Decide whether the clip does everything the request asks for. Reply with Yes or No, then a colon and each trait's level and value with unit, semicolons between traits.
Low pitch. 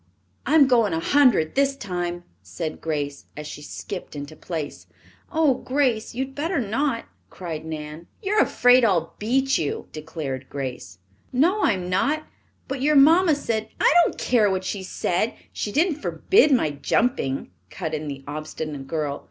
No: high, 195 Hz